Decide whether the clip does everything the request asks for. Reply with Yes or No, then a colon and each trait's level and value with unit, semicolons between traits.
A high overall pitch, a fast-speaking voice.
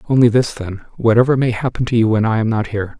No: low, 115 Hz; fast, 260 wpm